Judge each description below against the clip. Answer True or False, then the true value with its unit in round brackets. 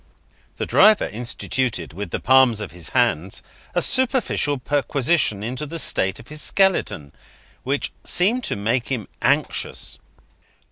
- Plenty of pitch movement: True (6.5 semitones)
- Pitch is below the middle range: True (130 Hz)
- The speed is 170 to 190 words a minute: False (135 wpm)